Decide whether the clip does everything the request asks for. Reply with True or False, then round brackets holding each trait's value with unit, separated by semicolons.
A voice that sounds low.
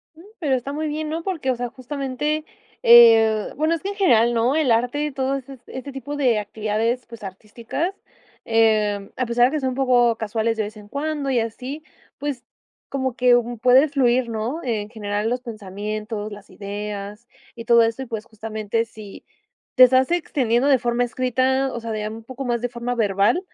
False (240 Hz)